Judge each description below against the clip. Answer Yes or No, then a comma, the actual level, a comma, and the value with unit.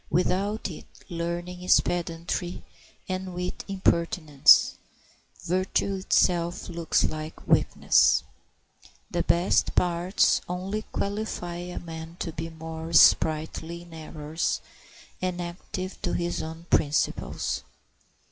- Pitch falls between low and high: Yes, medium, 175 Hz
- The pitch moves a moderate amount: No, narrow, 1.9 semitones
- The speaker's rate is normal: No, slow, 105 wpm